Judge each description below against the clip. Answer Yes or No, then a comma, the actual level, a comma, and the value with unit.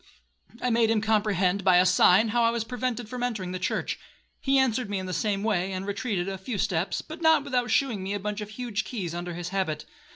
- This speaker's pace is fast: Yes, fast, 235 wpm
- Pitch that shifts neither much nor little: Yes, average, 4.4 semitones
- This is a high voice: Yes, high, 210 Hz